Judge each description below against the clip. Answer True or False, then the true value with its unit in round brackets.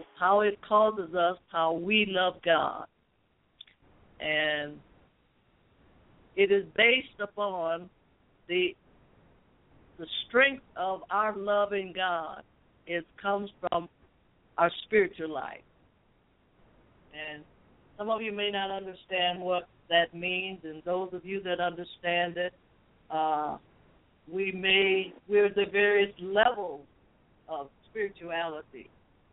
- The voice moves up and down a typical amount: True (3.2 semitones)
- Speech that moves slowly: True (105 wpm)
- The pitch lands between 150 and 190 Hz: True (185 Hz)